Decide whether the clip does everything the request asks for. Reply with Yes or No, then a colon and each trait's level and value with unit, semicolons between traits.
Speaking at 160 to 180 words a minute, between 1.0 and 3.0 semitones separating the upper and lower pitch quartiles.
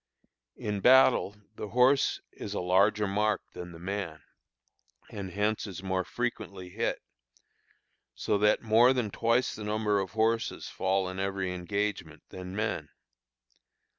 No: slow, 135 wpm; narrow, 2.5 semitones